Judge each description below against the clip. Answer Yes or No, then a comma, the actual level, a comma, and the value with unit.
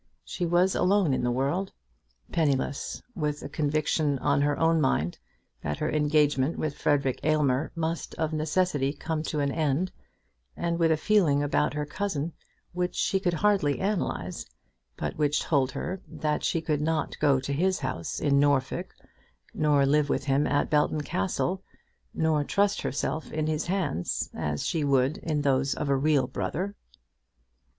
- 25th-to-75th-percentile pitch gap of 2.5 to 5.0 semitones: Yes, average, 2.8 semitones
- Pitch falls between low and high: Yes, medium, 150 Hz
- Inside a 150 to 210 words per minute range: Yes, average, 160 wpm